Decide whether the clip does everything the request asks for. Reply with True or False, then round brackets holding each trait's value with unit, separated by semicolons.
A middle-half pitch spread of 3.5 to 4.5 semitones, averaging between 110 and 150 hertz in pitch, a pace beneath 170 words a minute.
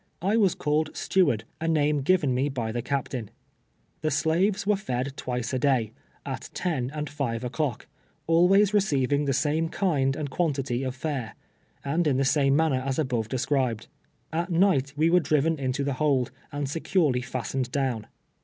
False (3.8 semitones; 140 Hz; 180 wpm)